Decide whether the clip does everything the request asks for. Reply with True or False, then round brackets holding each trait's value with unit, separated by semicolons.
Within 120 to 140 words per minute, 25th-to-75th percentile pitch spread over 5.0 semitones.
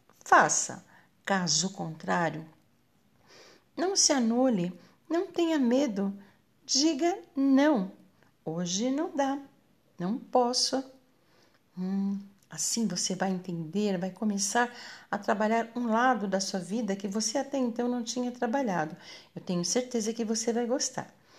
True (125 wpm; 5.5 semitones)